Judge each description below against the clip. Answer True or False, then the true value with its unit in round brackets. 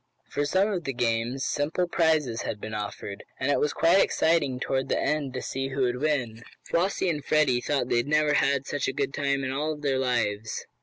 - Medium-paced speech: False (215 wpm)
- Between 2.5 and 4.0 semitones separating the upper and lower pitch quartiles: True (3.5 semitones)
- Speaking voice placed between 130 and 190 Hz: True (140 Hz)